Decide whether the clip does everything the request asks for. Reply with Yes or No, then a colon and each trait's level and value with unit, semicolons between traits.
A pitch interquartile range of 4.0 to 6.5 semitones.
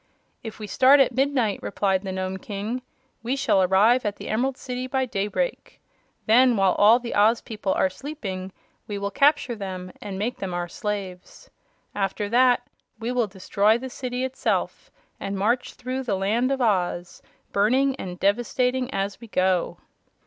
Yes: average, 4.4 semitones